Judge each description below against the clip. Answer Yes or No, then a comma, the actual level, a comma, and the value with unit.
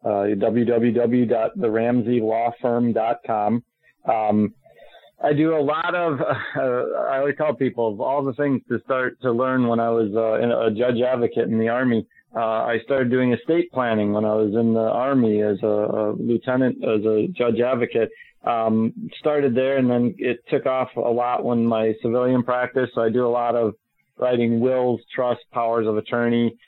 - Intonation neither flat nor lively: No, narrow, 2.2 semitones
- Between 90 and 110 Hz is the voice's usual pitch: No, low, 120 Hz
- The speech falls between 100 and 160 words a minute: No, average, 170 wpm